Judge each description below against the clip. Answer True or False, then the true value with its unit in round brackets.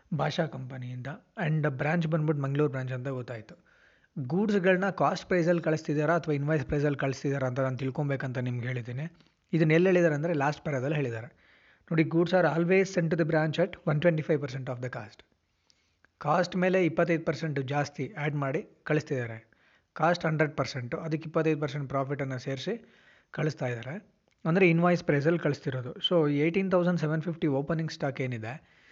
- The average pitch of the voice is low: False (155 Hz)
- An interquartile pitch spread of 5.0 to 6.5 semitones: False (3.8 semitones)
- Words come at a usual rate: False (155 wpm)